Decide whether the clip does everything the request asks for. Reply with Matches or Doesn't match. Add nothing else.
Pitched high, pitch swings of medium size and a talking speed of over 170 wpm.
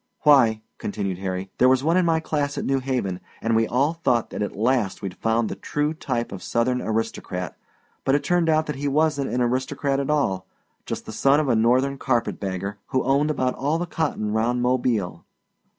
Doesn't match